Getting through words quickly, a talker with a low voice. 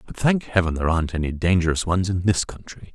Yes: fast, 225 wpm; very low, 90 Hz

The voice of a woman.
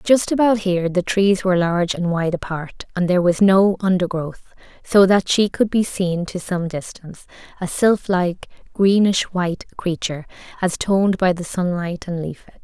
Yes: female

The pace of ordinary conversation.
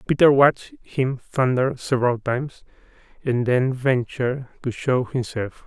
No: slow, 125 wpm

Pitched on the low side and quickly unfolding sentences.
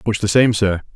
Yes: low, 105 Hz; fast, 255 wpm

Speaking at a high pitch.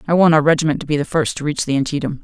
No: medium, 150 Hz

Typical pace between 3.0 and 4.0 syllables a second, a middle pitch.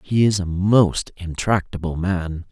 No: 3.8 syllables/s; very low, 90 Hz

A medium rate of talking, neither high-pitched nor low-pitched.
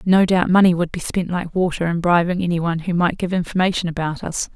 No: fast, 235 wpm; medium, 175 Hz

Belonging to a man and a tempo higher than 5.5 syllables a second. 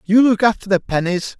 No: male; 5.4 syllables/s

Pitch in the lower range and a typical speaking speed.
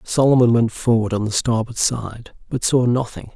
Yes: low, 115 Hz; average, 180 wpm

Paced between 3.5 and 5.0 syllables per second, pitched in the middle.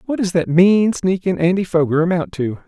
No: 5.2 syllables/s; medium, 175 Hz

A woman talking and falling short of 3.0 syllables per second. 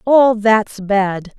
Yes: female; 2.4 syllables/s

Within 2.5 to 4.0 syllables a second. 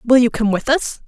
No: 5.1 syllables/s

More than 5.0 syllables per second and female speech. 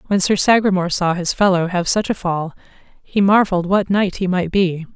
Yes: 5.4 syllables/s; female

